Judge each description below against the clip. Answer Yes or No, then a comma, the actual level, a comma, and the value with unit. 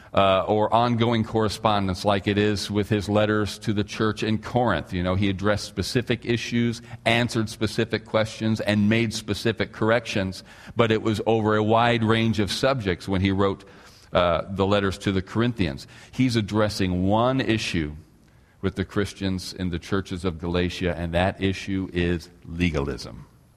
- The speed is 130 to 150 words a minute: No, average, 160 wpm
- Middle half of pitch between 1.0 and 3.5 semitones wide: Yes, average, 2.8 semitones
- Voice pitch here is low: Yes, low, 105 Hz